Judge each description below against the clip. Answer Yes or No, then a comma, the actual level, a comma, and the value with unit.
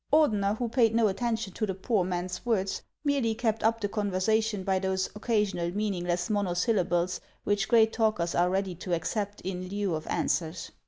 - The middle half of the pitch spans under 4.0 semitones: Yes, average, 3.4 semitones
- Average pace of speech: Yes, average, 175 wpm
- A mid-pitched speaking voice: No, high, 200 Hz